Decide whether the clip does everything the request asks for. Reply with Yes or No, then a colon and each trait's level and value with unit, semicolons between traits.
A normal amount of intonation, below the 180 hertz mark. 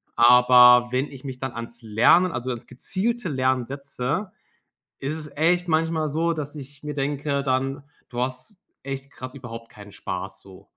Yes: average, 3.6 semitones; low, 135 Hz